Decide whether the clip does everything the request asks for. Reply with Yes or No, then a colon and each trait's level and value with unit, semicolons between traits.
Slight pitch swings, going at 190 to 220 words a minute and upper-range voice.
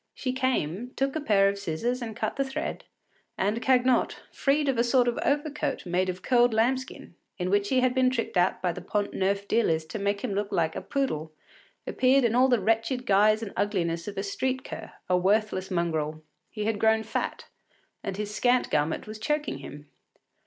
No: average, 5.0 semitones; average, 195 wpm; high, 215 Hz